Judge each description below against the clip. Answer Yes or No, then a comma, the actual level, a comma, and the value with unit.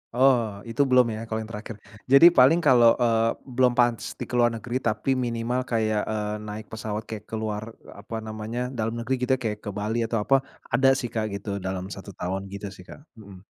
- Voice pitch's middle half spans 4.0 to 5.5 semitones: No, average, 2.7 semitones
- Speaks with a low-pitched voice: Yes, low, 115 Hz